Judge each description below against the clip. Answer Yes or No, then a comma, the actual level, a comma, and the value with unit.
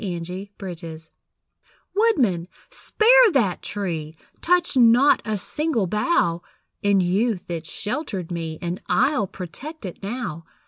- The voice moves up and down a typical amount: No, wide, 7.0 semitones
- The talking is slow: Yes, slow, 120 wpm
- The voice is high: Yes, high, 195 Hz